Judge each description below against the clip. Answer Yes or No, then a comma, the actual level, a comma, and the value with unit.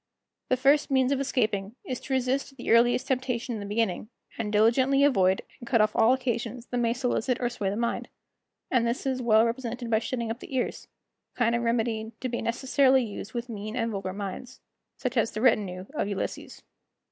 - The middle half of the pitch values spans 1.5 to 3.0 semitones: Yes, average, 2.7 semitones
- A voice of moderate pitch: No, high, 235 Hz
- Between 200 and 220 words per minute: Yes, fast, 205 wpm